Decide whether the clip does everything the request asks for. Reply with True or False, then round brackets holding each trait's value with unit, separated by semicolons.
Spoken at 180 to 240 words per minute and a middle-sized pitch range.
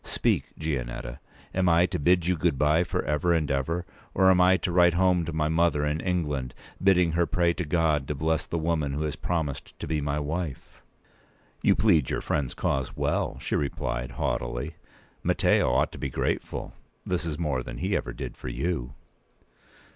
True (190 wpm; 3.4 semitones)